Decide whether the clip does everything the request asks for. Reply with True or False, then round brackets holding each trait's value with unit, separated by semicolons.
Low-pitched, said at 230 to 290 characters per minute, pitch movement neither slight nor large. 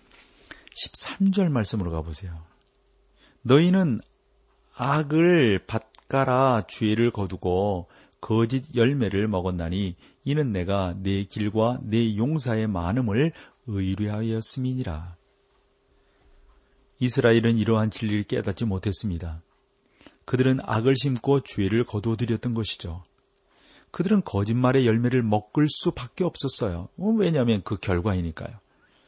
True (115 Hz; 250 characters per minute; 4.6 semitones)